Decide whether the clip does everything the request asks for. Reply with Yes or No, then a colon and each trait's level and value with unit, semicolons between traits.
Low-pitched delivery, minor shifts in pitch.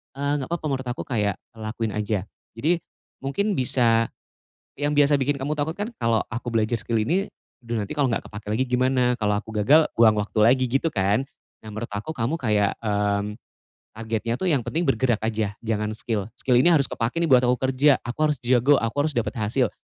No: low, 120 Hz; average, 4.2 semitones